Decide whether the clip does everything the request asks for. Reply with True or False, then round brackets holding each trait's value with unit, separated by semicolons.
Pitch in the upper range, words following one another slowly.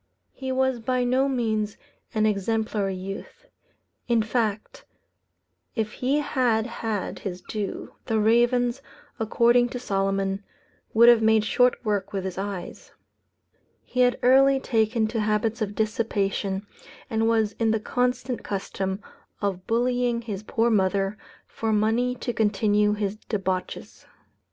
True (220 Hz; 130 wpm)